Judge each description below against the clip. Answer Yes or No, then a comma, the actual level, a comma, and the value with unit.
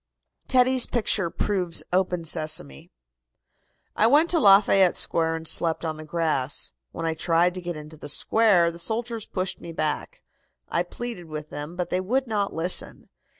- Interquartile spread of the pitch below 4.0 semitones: No, average, 4.6 semitones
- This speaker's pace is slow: No, average, 165 wpm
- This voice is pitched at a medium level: Yes, medium, 175 Hz